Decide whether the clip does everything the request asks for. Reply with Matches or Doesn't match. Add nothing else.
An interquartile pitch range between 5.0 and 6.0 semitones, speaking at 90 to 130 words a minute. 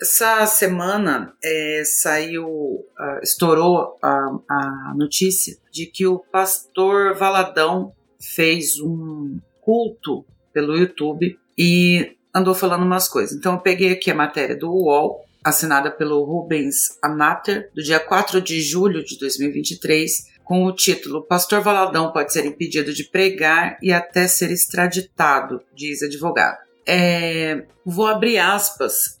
Doesn't match